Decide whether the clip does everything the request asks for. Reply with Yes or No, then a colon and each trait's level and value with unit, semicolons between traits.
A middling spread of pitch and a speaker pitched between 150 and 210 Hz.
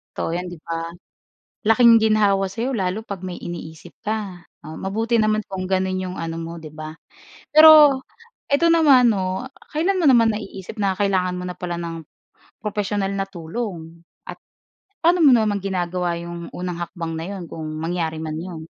Yes: average, 4.2 semitones; high, 190 Hz